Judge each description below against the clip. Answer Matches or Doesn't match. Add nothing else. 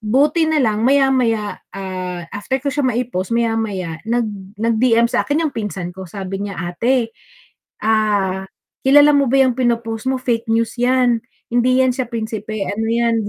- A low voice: Doesn't match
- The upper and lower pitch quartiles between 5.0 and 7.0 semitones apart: Doesn't match